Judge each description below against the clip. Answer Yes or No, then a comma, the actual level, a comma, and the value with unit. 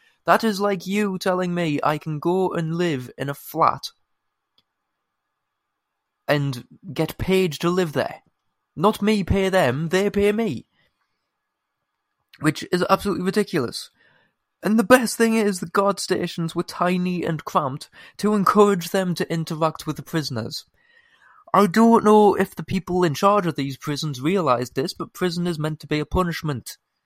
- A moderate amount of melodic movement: Yes, average, 4.3 semitones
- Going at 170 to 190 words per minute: No, average, 160 wpm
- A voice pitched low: No, medium, 180 Hz